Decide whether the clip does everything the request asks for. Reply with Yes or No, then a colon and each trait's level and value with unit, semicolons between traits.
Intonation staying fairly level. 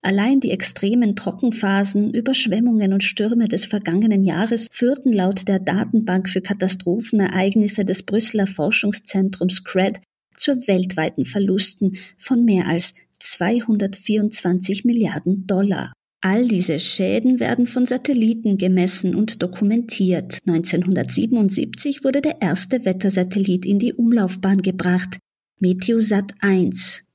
No: average, 3.3 semitones